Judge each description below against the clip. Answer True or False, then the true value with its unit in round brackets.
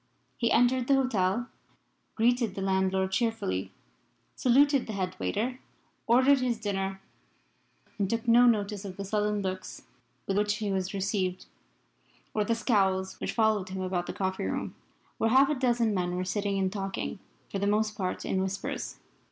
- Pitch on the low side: False (205 Hz)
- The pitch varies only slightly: False (3.5 semitones)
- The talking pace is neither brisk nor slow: True (165 wpm)